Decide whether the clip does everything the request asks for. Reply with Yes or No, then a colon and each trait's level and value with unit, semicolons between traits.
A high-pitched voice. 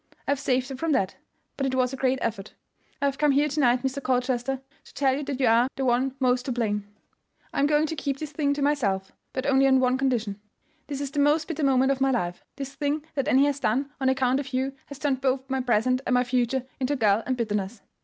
Yes: very high, 265 Hz